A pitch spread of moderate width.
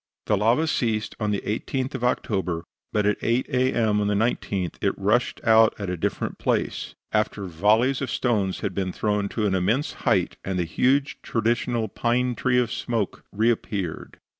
Yes: average, 3.3 semitones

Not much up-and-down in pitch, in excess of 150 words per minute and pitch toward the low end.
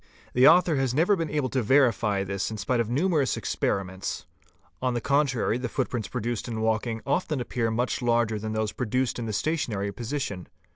No: average, 3.7 semitones; average, 185 wpm; low, 120 Hz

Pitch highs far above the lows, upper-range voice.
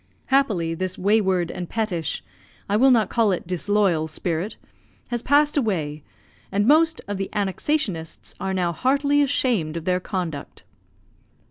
Yes: wide, 5.9 semitones; high, 195 Hz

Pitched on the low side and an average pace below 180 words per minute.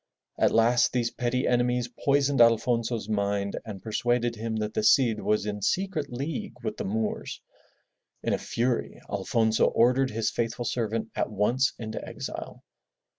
Yes: low, 115 Hz; average, 150 wpm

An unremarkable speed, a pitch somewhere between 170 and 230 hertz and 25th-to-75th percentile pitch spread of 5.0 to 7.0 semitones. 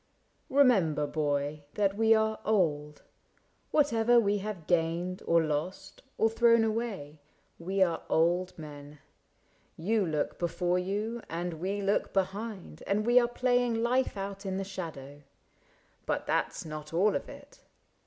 Yes: average, 145 wpm; high, 190 Hz; wide, 5.4 semitones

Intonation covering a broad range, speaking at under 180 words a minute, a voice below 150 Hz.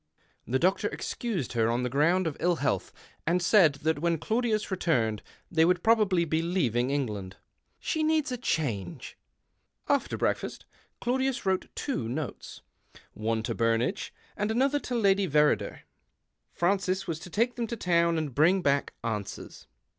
No: wide, 7.5 semitones; average, 160 wpm; medium, 170 Hz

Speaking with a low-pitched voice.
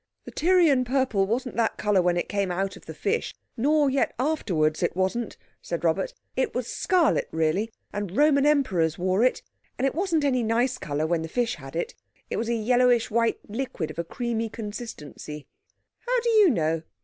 No: high, 230 Hz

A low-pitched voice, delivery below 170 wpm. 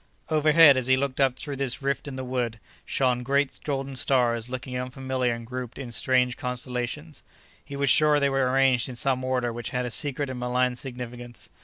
No: low, 130 Hz; average, 195 wpm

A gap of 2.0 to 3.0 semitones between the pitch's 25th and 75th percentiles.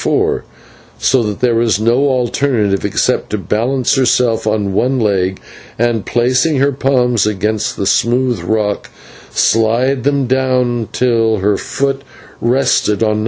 No: average, 3.4 semitones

